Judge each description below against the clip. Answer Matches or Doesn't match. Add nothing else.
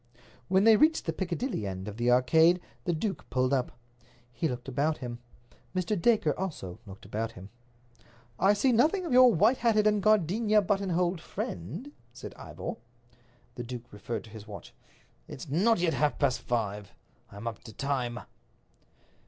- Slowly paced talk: Doesn't match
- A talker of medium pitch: Matches